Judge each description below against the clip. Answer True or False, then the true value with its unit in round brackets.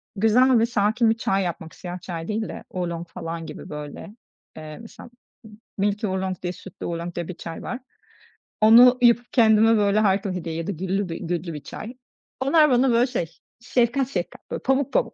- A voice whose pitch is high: True (200 Hz)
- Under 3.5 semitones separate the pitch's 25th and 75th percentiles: False (5.2 semitones)